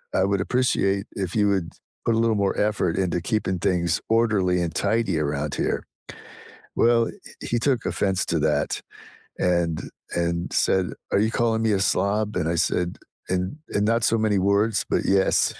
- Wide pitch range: No, average, 3.7 semitones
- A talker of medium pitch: No, low, 100 Hz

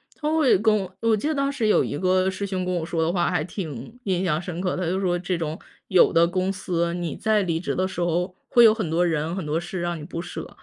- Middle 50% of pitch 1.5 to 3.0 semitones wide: Yes, narrow, 2.4 semitones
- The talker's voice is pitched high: No, medium, 180 Hz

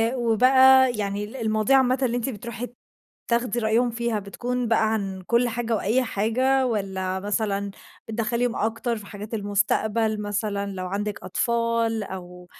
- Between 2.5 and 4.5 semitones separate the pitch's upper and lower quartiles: Yes, average, 2.9 semitones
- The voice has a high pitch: Yes, high, 220 Hz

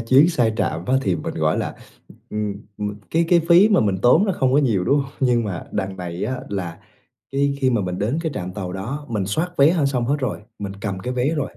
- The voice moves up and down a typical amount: No, wide, 6.3 semitones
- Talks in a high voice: No, low, 120 Hz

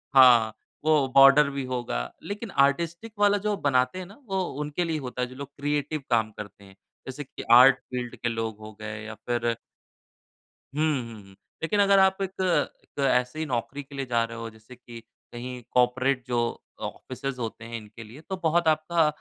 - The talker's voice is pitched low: Yes, low, 130 Hz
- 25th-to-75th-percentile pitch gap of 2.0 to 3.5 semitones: No, average, 4.8 semitones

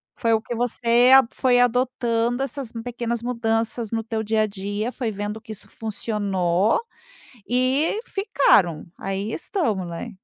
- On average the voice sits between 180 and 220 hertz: No, high, 230 Hz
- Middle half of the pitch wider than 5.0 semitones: No, narrow, 2.6 semitones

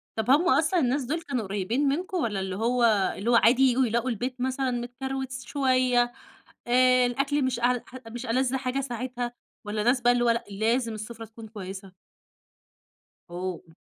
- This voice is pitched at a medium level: No, high, 245 Hz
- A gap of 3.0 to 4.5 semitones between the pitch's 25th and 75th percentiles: No, narrow, 2.5 semitones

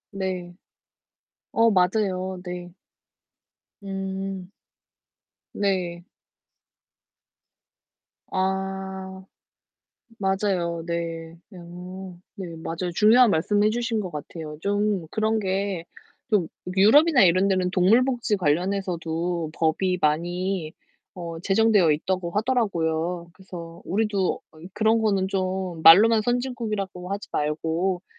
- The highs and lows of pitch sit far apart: No, average, 2.9 semitones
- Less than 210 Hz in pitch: Yes, high, 190 Hz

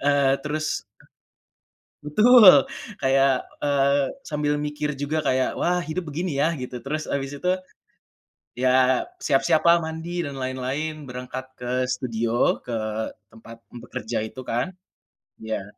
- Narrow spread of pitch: No, average, 3.3 semitones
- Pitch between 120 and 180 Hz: Yes, medium, 140 Hz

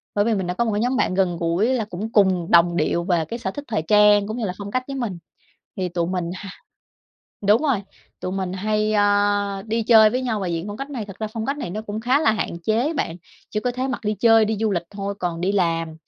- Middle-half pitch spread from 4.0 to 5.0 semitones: No, average, 3.6 semitones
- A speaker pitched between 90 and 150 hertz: No, high, 205 Hz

